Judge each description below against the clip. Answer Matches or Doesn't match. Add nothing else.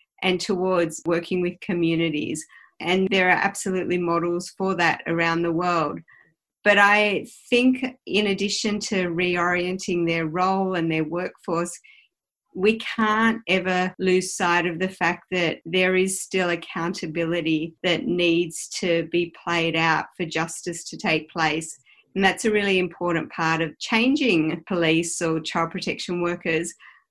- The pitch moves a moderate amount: Doesn't match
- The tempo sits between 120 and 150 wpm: Matches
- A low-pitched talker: Doesn't match